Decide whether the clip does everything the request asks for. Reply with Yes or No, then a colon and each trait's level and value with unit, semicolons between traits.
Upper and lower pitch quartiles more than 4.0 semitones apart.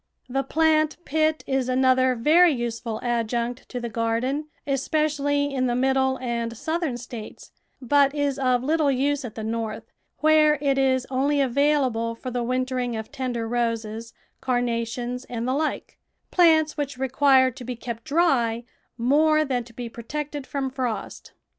No: average, 3.3 semitones